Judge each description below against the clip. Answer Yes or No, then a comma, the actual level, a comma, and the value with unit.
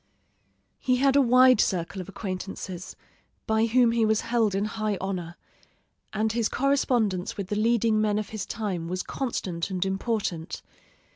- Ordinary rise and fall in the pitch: Yes, average, 3.5 semitones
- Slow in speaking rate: No, average, 155 wpm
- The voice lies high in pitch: Yes, high, 215 Hz